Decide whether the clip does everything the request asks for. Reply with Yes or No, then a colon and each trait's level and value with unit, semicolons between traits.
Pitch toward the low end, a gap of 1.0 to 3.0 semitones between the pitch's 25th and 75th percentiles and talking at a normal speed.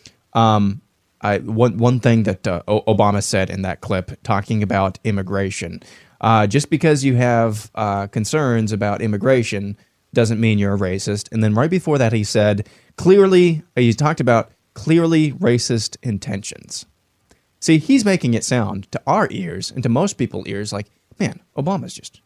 No: low, 110 Hz; average, 3.8 semitones; average, 165 wpm